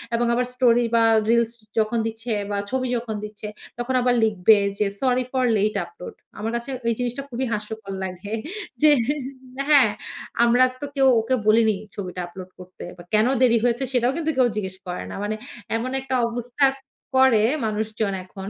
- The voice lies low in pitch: No, high, 230 Hz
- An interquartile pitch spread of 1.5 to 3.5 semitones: Yes, average, 3.0 semitones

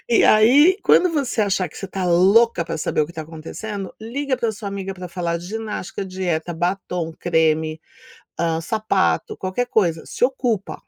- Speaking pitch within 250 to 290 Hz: No, high, 190 Hz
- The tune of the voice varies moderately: Yes, average, 4.6 semitones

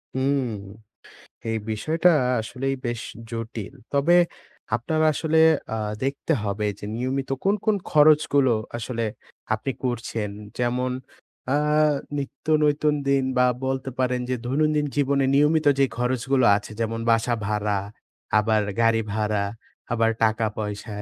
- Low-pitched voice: Yes, low, 125 Hz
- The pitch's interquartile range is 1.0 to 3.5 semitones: No, average, 3.9 semitones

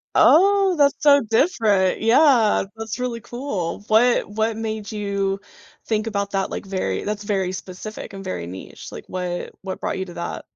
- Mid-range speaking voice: No, high, 210 Hz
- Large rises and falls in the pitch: No, average, 3.4 semitones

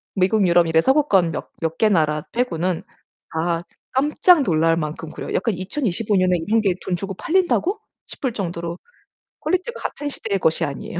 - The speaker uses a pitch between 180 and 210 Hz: Yes, medium, 185 Hz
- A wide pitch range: Yes, wide, 6.8 semitones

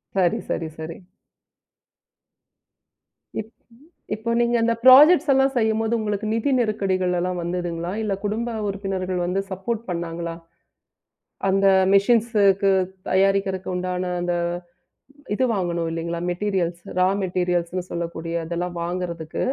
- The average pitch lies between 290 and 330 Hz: No, medium, 185 Hz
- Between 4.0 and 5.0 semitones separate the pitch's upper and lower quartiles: No, average, 3.4 semitones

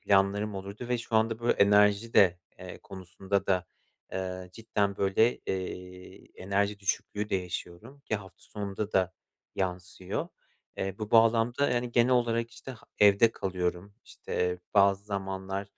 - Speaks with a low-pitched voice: Yes, low, 100 Hz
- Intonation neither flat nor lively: Yes, average, 3.0 semitones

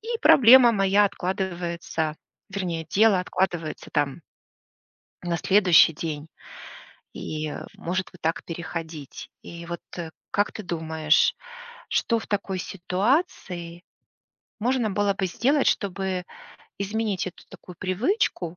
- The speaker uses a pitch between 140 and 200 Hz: Yes, medium, 185 Hz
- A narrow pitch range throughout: No, average, 3.4 semitones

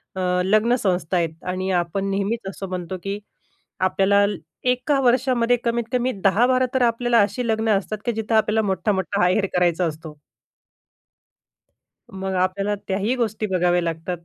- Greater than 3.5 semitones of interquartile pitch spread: Yes, average, 4.1 semitones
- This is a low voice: No, high, 200 Hz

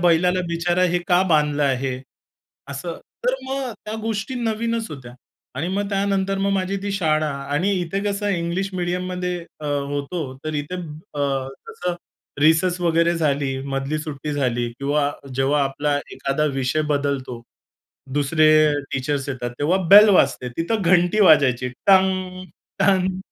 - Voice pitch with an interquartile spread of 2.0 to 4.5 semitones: No, average, 4.9 semitones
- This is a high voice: No, medium, 165 Hz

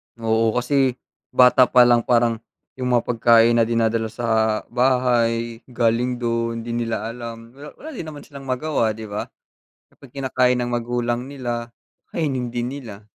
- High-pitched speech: No, low, 120 Hz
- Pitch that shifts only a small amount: Yes, narrow, 1.6 semitones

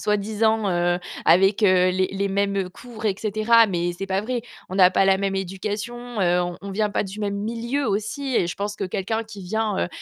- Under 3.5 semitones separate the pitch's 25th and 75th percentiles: Yes, narrow, 2.5 semitones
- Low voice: No, high, 200 Hz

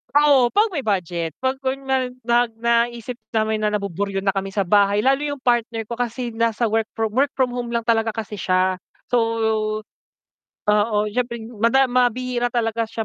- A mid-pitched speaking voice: No, high, 230 Hz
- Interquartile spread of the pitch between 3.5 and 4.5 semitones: No, average, 3.0 semitones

